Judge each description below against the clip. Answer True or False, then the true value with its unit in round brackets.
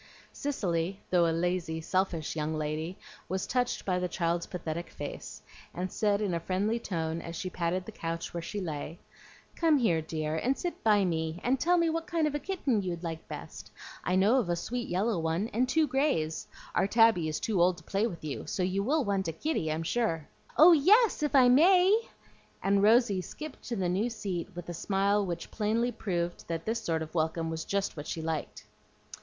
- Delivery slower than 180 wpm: False (205 wpm)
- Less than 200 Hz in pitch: True (185 Hz)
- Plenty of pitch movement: True (6.0 semitones)